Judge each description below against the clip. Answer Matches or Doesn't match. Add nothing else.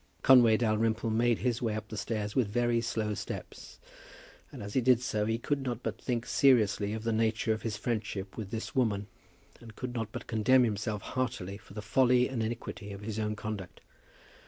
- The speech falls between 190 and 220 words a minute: Matches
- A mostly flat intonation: Matches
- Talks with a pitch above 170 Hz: Doesn't match